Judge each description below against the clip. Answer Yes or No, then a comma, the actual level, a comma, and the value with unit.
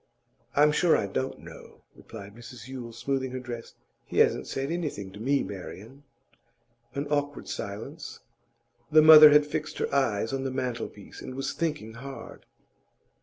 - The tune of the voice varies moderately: Yes, average, 4.1 semitones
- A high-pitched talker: No, low, 135 Hz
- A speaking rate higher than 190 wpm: No, average, 155 wpm